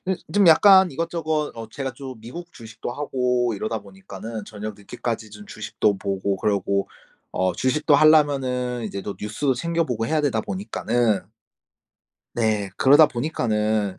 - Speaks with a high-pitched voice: No, low, 120 Hz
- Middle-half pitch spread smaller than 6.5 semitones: Yes, wide, 5.5 semitones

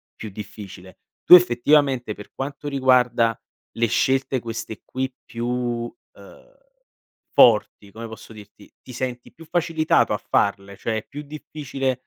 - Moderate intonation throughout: Yes, average, 3.7 semitones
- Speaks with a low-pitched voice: Yes, low, 125 Hz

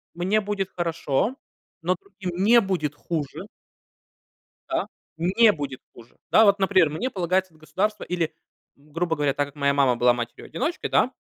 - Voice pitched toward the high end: No, medium, 175 Hz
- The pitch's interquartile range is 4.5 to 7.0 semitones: Yes, average, 5.2 semitones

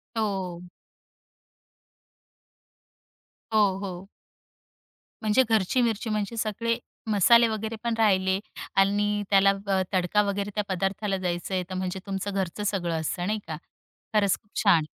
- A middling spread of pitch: No, narrow, 2.3 semitones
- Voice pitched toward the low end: No, high, 200 Hz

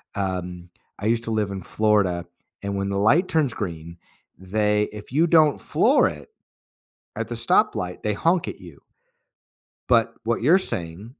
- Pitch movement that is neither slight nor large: Yes, average, 4.4 semitones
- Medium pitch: No, low, 105 Hz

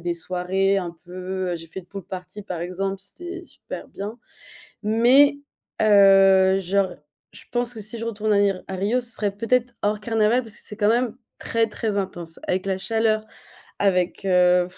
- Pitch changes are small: No, average, 3.3 semitones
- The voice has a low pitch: No, high, 200 Hz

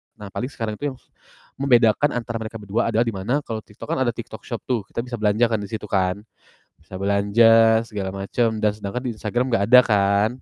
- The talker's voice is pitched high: No, low, 110 Hz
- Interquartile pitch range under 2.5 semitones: No, average, 2.8 semitones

